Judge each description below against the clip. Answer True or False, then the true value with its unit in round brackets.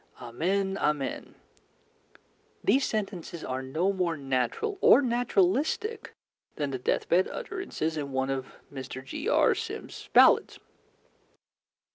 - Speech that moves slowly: True (110 wpm)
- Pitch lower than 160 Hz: False (170 Hz)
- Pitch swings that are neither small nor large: False (8.3 semitones)